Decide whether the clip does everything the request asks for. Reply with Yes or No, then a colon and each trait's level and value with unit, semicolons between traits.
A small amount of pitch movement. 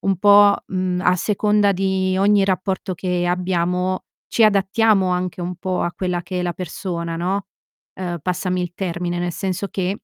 Yes: narrow, 1.6 semitones